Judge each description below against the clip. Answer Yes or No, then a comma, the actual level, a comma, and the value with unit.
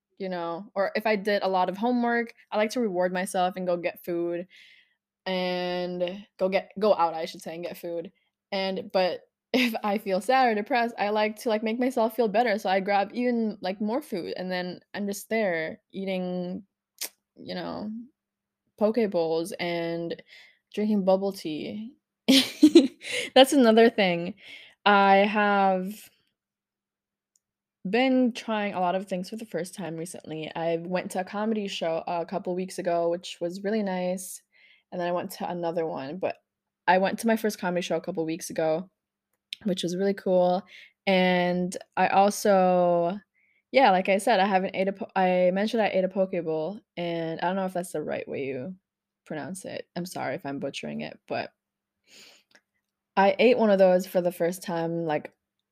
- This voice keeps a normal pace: Yes, average, 180 wpm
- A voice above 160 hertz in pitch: Yes, high, 190 Hz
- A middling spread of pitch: Yes, average, 3.4 semitones